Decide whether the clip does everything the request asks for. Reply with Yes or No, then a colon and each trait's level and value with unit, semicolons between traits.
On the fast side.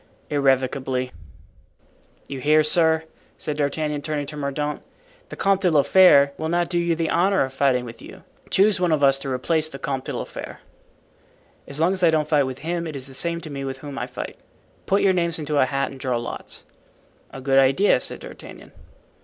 Yes: fast, 210 wpm